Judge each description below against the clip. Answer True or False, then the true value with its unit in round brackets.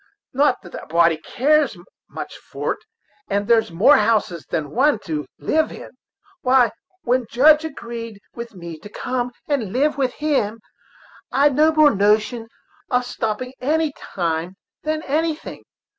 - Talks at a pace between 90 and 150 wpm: True (145 wpm)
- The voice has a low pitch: False (245 Hz)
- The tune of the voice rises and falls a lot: True (6.1 semitones)